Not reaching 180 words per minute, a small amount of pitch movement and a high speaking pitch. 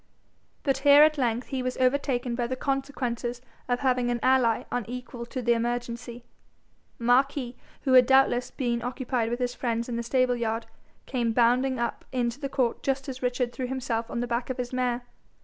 No: average, 185 wpm; narrow, 1.6 semitones; high, 245 Hz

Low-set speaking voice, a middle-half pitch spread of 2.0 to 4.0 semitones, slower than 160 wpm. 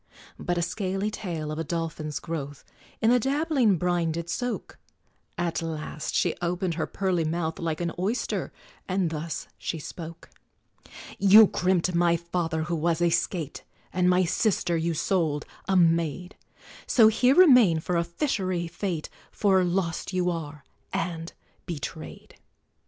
No: medium, 175 Hz; narrow, 2.5 semitones; average, 145 wpm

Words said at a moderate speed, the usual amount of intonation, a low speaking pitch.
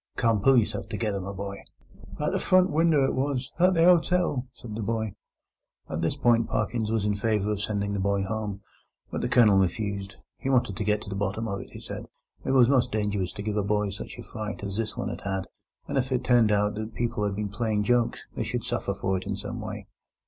No: fast, 235 wpm; average, 3.2 semitones; low, 105 Hz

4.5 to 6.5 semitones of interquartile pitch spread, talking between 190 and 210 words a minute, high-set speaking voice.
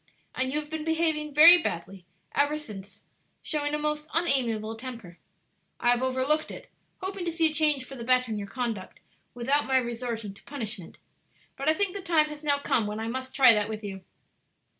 Yes: average, 5.2 semitones; average, 200 wpm; very high, 260 Hz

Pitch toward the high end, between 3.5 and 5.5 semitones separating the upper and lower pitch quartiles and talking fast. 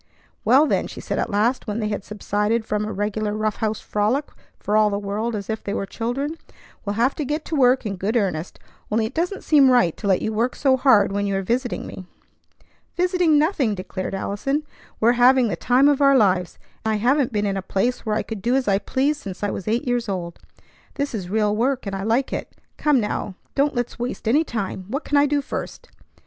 Yes: high, 225 Hz; average, 4.6 semitones; fast, 230 wpm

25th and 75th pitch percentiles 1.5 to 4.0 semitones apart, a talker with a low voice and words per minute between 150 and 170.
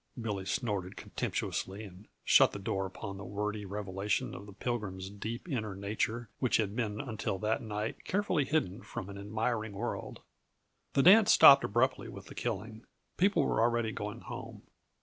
Yes: average, 3.0 semitones; low, 105 Hz; average, 165 wpm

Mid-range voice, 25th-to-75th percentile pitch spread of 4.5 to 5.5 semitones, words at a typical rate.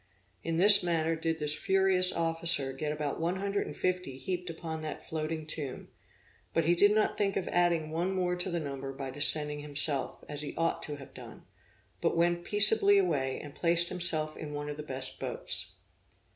No: medium, 165 Hz; average, 3.2 semitones; average, 190 wpm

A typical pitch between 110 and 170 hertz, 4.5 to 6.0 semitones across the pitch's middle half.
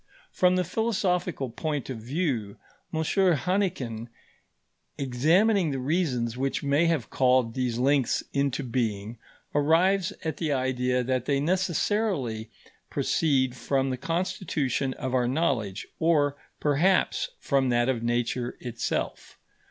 Yes: low, 135 Hz; average, 5.2 semitones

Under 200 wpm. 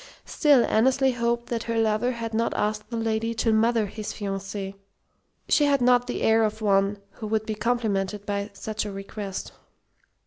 Yes: average, 175 wpm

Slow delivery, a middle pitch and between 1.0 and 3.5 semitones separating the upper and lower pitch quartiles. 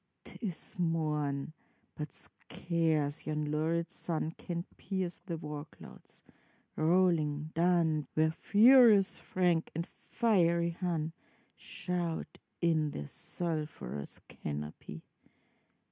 Yes: slow, 100 wpm; medium, 165 Hz; narrow, 2.6 semitones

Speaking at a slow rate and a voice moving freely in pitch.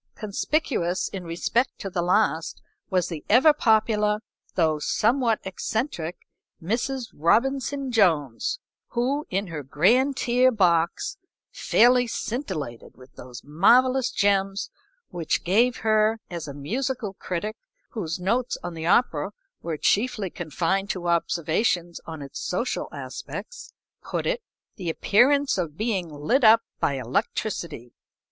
Yes: slow, 125 wpm; wide, 6.3 semitones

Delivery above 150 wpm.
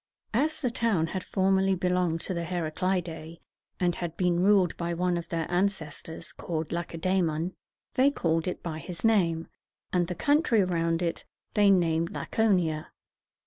Yes: average, 170 wpm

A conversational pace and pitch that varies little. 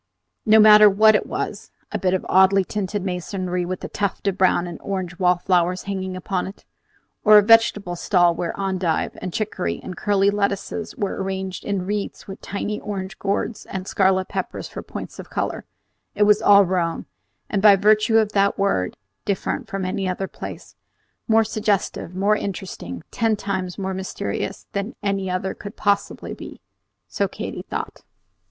Yes: average, 170 wpm; narrow, 1.9 semitones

